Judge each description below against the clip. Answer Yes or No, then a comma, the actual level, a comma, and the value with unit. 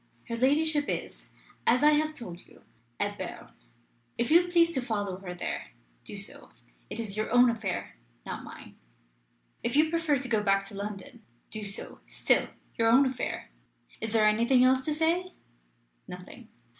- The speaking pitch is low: No, high, 240 Hz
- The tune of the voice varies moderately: No, wide, 6.0 semitones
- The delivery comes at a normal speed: Yes, average, 170 wpm